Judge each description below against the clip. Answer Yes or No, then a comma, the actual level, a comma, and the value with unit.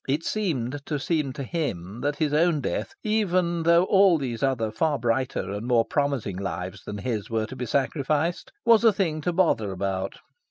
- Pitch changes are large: Yes, wide, 6.9 semitones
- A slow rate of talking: No, average, 190 wpm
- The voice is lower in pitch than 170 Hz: Yes, medium, 140 Hz